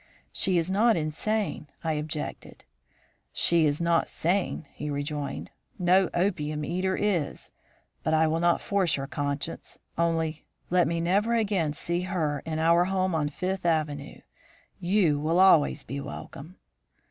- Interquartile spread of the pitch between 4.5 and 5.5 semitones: No, average, 3.5 semitones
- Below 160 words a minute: Yes, average, 145 wpm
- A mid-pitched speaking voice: Yes, medium, 165 Hz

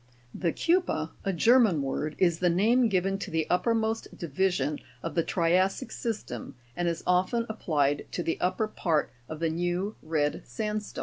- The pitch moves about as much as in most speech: Yes, average, 4.8 semitones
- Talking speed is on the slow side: No, average, 180 wpm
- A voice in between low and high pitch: Yes, medium, 180 Hz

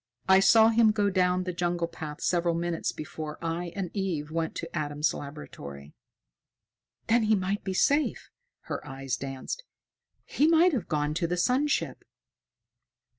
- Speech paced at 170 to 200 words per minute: No, average, 155 wpm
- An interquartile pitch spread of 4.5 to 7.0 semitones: Yes, average, 4.9 semitones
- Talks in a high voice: No, medium, 175 Hz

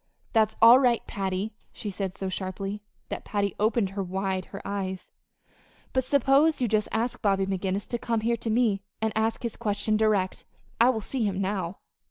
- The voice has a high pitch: Yes, high, 210 Hz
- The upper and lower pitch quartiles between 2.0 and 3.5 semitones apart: Yes, average, 3.0 semitones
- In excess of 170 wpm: Yes, average, 180 wpm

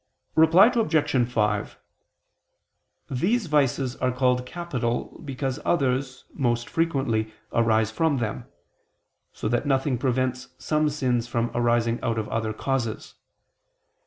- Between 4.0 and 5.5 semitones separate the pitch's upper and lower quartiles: No, average, 3.6 semitones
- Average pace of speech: No, slow, 115 wpm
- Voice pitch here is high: No, low, 125 Hz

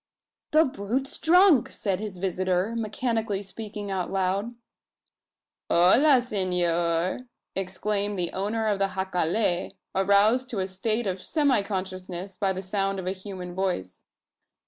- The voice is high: Yes, high, 195 Hz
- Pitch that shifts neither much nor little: Yes, average, 3.2 semitones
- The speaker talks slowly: Yes, slow, 125 wpm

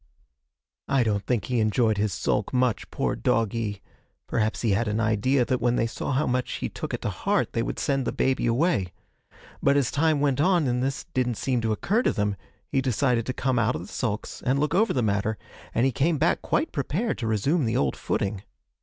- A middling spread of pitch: Yes, average, 4.0 semitones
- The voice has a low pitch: Yes, low, 125 Hz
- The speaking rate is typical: No, fast, 220 wpm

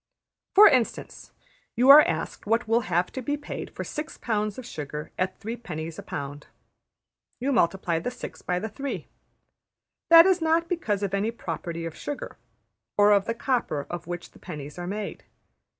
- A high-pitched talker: Yes, high, 210 Hz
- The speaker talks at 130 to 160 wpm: No, average, 175 wpm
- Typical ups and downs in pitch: No, wide, 7.1 semitones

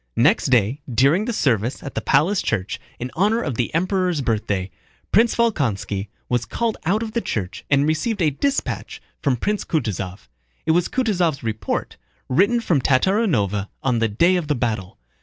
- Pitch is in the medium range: Yes, medium, 145 Hz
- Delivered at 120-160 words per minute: No, average, 170 wpm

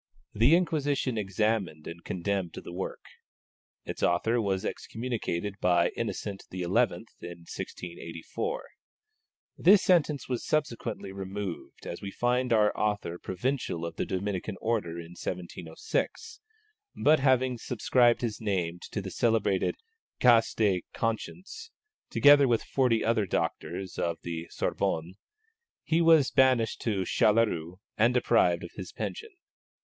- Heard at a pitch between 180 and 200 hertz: No, low, 105 Hz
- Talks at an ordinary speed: No, slow, 125 wpm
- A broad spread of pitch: Yes, wide, 5.7 semitones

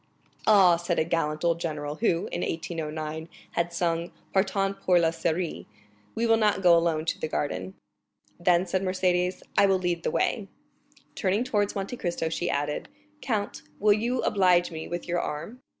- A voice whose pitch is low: No, medium, 175 Hz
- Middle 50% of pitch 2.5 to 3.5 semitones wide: Yes, average, 3.0 semitones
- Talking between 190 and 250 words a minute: No, average, 165 wpm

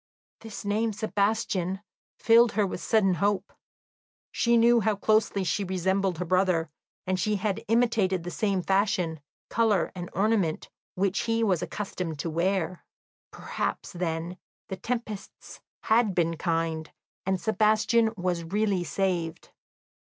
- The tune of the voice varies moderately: Yes, average, 3.5 semitones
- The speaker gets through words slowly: Yes, slow, 130 wpm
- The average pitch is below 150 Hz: No, high, 195 Hz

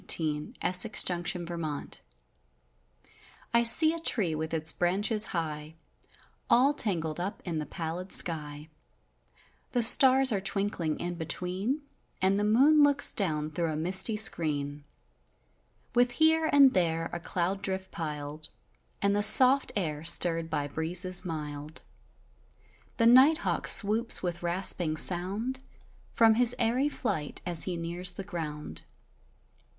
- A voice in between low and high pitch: Yes, medium, 180 Hz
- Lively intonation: Yes, wide, 5.8 semitones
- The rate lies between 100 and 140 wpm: Yes, slow, 135 wpm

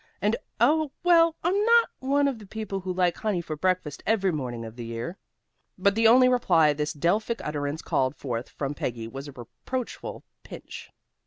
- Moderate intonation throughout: No, wide, 8.5 semitones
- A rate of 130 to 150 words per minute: No, average, 180 wpm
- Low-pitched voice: No, medium, 185 Hz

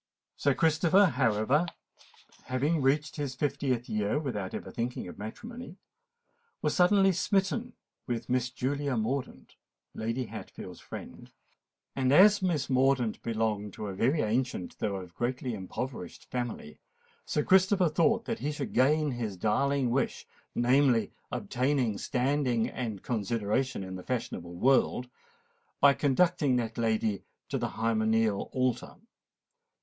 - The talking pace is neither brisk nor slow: No, slow, 125 wpm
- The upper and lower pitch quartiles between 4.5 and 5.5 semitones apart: Yes, average, 4.8 semitones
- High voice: No, low, 130 Hz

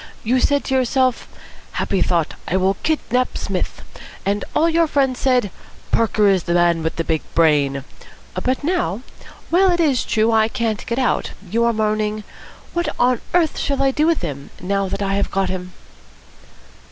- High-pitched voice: Yes, high, 220 Hz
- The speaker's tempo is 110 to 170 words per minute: No, average, 180 wpm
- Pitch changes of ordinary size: No, wide, 6.0 semitones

